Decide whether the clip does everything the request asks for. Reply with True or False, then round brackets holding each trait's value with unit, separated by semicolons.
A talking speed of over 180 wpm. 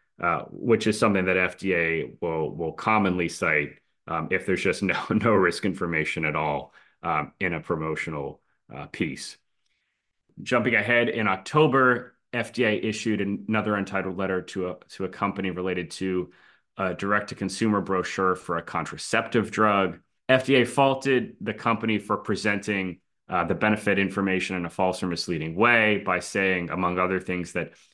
False (160 wpm)